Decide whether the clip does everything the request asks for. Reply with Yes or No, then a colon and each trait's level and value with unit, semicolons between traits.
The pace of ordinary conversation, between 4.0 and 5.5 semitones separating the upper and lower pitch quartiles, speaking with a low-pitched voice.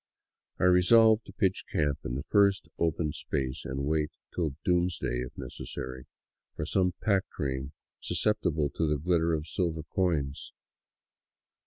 Yes: average, 145 wpm; average, 4.4 semitones; very low, 80 Hz